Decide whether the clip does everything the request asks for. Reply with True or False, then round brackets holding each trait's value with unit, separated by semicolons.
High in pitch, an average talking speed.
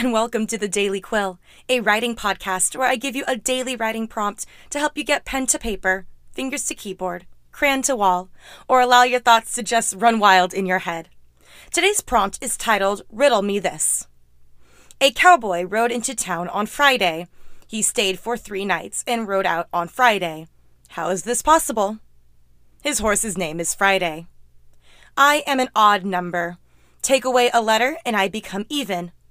True (210 Hz; 180 wpm)